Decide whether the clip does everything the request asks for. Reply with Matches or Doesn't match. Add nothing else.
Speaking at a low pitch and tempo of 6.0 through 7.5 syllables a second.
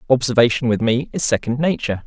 Matches